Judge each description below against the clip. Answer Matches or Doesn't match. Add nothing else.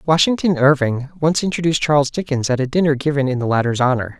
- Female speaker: Doesn't match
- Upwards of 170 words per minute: Matches